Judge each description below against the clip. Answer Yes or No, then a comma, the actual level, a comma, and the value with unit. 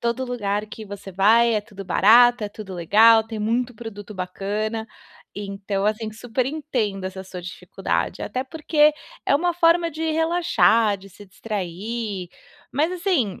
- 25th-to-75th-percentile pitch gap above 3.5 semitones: Yes, average, 4.0 semitones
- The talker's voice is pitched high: Yes, high, 220 Hz